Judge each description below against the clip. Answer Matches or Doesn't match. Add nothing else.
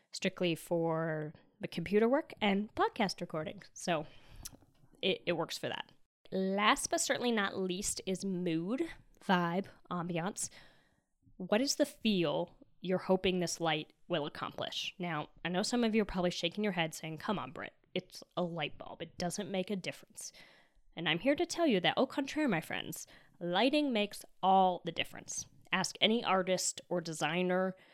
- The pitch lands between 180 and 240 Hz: Matches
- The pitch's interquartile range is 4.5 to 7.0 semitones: Doesn't match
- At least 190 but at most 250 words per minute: Doesn't match